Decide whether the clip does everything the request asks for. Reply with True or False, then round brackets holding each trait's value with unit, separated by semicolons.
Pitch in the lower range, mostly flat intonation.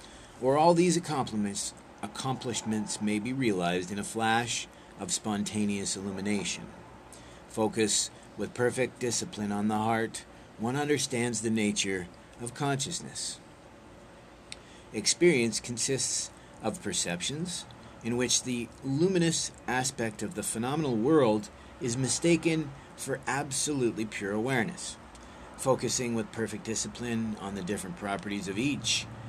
False (115 Hz; 3.3 semitones)